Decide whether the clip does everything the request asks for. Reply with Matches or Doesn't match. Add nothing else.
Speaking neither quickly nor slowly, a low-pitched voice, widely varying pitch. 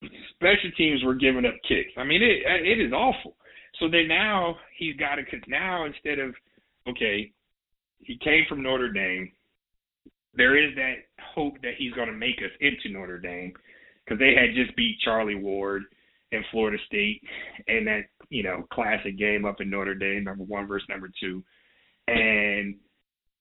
Matches